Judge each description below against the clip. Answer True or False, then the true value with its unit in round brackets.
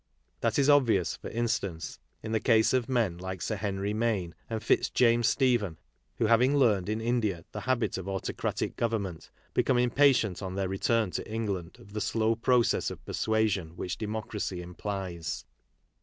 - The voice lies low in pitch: True (110 Hz)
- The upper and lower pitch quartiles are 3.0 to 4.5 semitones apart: True (3.6 semitones)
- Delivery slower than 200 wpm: True (160 wpm)